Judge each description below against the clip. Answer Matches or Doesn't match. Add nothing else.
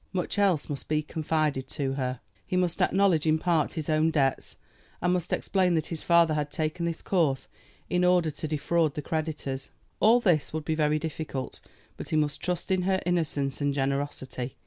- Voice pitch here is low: Doesn't match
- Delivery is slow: Doesn't match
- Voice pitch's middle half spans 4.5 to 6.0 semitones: Doesn't match